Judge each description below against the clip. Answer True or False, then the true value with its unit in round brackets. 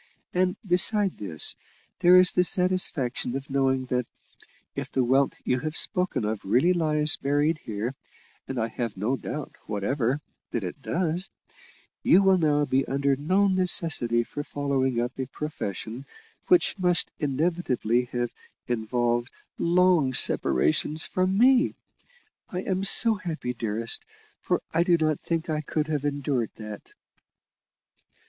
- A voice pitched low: False (145 Hz)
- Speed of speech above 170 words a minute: False (140 wpm)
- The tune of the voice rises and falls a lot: True (6.3 semitones)